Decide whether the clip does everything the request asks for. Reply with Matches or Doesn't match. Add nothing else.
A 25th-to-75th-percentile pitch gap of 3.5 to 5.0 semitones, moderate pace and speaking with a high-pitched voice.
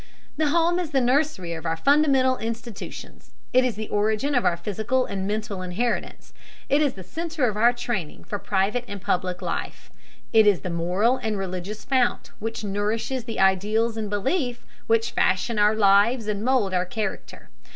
Matches